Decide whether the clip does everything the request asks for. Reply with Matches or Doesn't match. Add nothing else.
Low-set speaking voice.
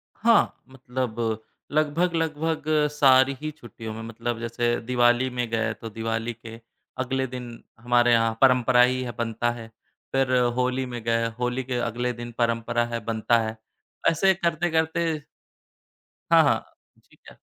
Matches